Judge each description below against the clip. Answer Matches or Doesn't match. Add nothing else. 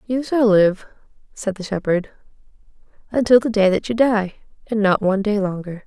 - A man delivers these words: Doesn't match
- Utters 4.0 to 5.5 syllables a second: Matches